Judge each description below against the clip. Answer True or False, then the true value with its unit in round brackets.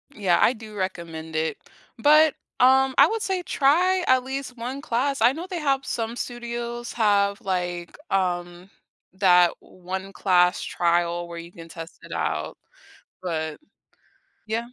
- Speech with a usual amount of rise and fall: False (7.0 semitones)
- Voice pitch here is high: True (210 Hz)